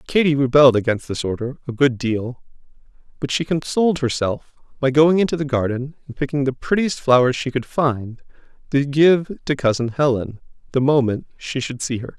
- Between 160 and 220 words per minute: Yes, average, 175 wpm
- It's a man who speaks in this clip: Yes, male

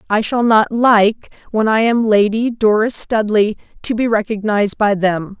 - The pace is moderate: Yes, average, 165 wpm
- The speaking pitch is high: Yes, high, 215 Hz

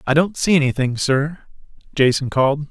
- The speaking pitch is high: No, medium, 145 Hz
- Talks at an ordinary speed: Yes, average, 155 wpm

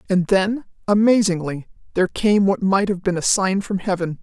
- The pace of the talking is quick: No, average, 185 wpm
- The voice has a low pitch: No, high, 190 Hz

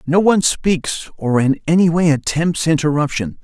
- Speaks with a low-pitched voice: No, medium, 155 Hz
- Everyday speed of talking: Yes, average, 155 wpm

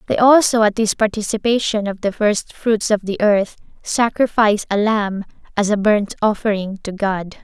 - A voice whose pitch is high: Yes, high, 210 Hz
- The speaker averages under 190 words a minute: Yes, average, 170 wpm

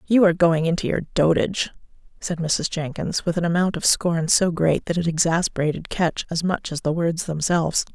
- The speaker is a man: No, female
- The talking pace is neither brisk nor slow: Yes, average, 195 wpm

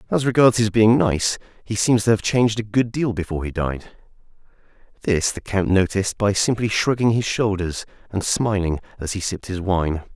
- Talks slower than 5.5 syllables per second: Yes, 5.3 syllables/s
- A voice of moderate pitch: No, low, 105 Hz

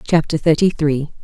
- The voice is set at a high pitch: No, medium, 155 Hz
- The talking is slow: No, average, 145 wpm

